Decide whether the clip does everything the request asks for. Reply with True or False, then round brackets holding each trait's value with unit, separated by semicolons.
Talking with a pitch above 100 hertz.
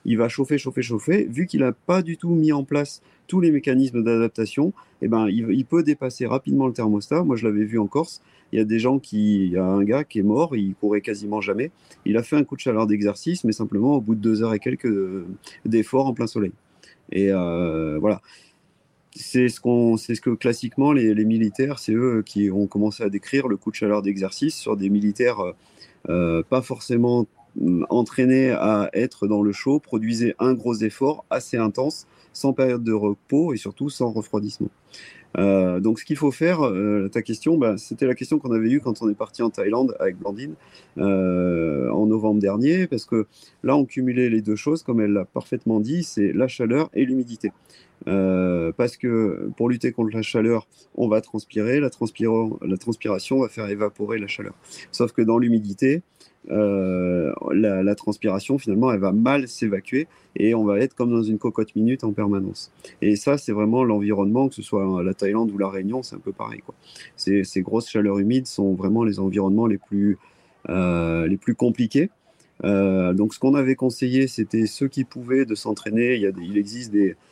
True (110 Hz)